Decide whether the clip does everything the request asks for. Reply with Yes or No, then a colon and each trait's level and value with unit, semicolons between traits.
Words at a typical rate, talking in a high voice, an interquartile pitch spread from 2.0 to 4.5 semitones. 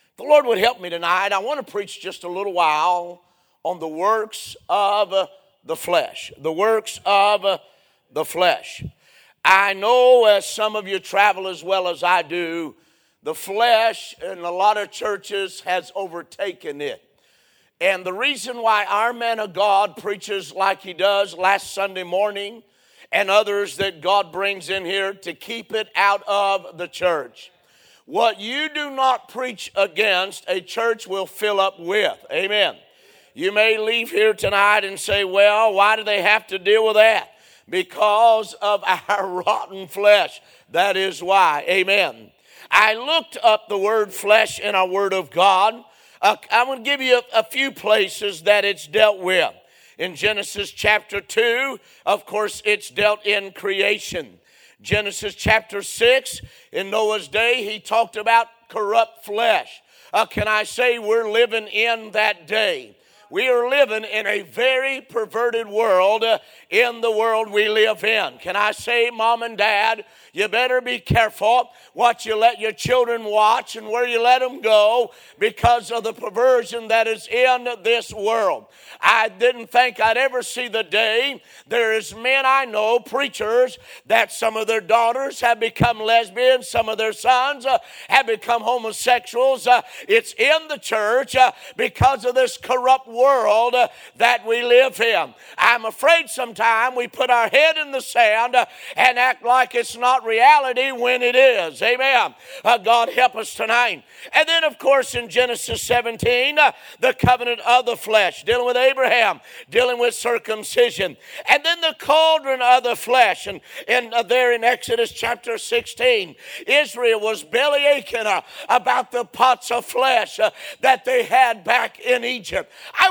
Yes: average, 165 wpm; high, 225 Hz; average, 3.6 semitones